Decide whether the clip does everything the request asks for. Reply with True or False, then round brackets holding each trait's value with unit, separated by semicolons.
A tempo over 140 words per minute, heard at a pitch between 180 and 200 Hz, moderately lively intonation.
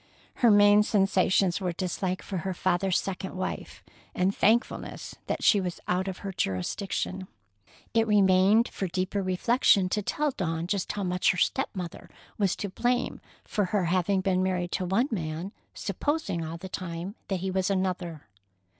False (165 wpm; 190 Hz; 2.0 semitones)